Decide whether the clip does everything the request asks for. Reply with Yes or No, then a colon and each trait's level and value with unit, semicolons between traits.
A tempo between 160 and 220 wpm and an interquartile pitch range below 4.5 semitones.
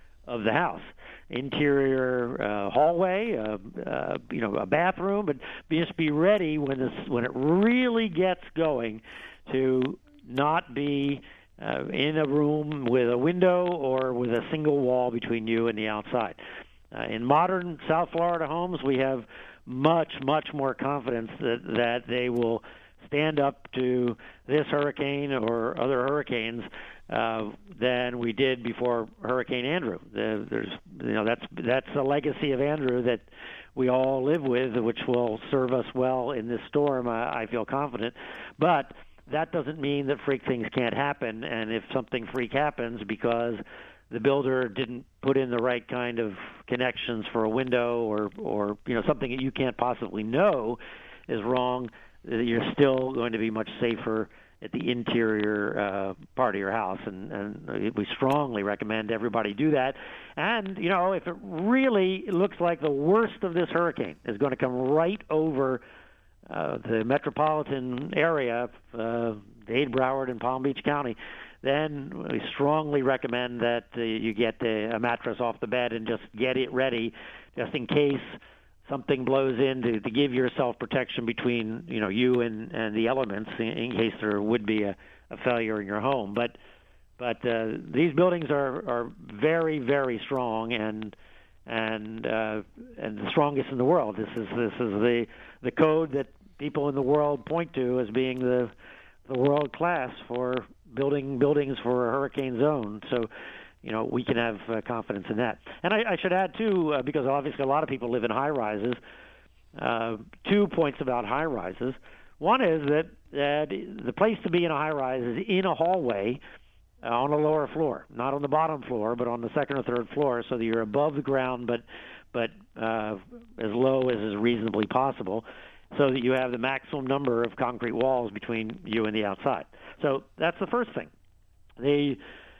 Yes: average, 175 wpm; average, 3.9 semitones